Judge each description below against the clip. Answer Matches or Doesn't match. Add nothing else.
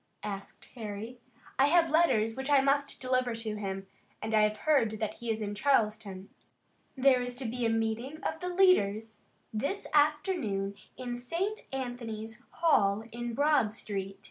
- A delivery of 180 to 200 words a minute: Doesn't match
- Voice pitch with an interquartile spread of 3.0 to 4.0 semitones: Doesn't match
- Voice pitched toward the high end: Matches